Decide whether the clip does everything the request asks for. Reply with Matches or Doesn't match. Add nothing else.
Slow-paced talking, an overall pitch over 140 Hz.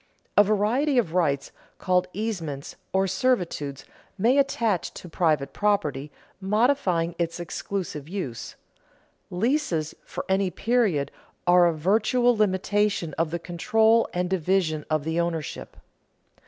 Matches